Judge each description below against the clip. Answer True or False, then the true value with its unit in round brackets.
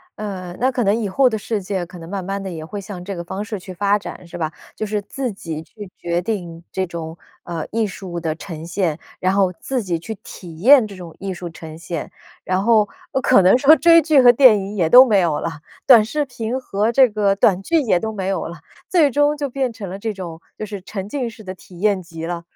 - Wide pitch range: False (4.4 semitones)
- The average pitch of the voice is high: True (195 Hz)